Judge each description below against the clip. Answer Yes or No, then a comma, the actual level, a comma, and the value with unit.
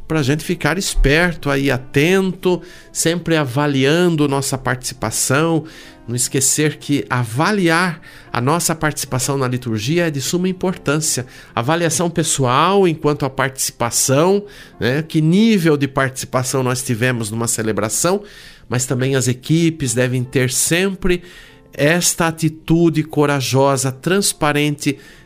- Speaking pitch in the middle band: Yes, medium, 145 Hz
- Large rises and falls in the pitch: No, average, 4.1 semitones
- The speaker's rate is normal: No, slow, 115 wpm